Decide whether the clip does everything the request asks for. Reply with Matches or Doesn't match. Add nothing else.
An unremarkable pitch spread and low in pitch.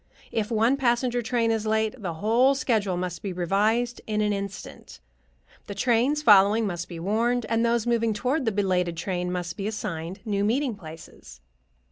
Doesn't match